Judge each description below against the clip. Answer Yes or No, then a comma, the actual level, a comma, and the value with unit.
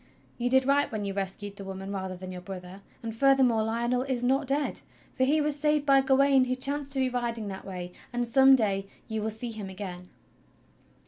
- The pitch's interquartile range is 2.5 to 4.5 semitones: No, wide, 5.4 semitones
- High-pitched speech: Yes, high, 235 Hz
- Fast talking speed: Yes, fast, 210 wpm